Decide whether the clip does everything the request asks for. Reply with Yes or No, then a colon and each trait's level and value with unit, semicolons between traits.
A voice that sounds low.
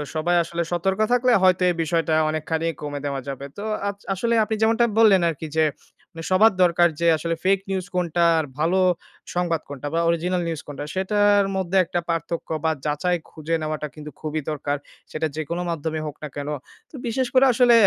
No: medium, 170 Hz